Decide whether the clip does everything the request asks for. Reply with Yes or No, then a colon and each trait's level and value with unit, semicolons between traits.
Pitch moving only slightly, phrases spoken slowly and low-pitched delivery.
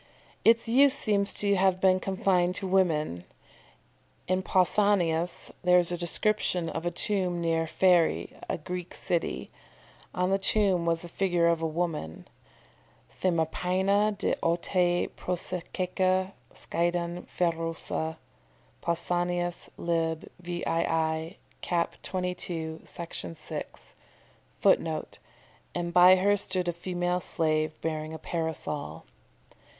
No: narrow, 2.1 semitones; slow, 115 wpm; medium, 175 Hz